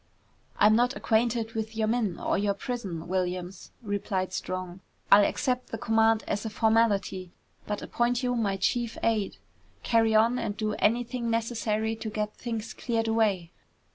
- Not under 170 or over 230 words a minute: No, average, 155 wpm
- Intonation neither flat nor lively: No, narrow, 2.3 semitones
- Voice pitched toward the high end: Yes, high, 220 Hz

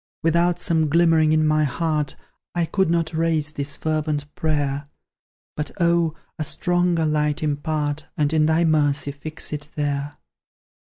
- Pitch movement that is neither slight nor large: No, narrow, 1.9 semitones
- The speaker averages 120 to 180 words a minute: Yes, average, 145 wpm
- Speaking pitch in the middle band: Yes, medium, 155 Hz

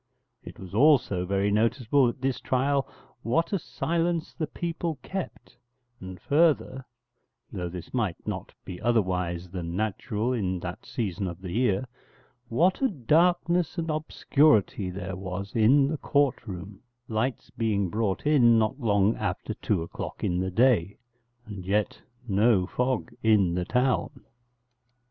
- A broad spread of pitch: Yes, wide, 6.5 semitones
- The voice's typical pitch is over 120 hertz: No, low, 110 Hz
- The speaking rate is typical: Yes, average, 145 wpm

